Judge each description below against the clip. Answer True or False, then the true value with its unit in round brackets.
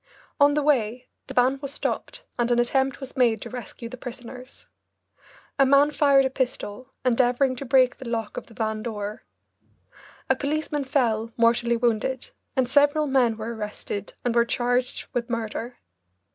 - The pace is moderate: True (165 wpm)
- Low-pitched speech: False (250 Hz)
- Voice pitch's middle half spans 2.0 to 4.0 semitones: True (2.6 semitones)